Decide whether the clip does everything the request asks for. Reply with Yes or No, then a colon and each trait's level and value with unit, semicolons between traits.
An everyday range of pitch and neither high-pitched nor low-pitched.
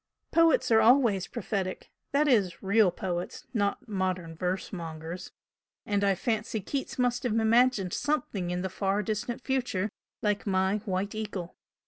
No: average, 3.7 semitones; high, 205 Hz